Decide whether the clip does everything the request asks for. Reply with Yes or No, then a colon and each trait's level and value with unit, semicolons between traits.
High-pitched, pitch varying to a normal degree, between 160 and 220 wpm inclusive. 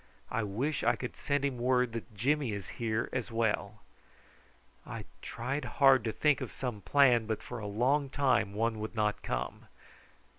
No: low, 120 Hz; average, 3.7 semitones; average, 175 wpm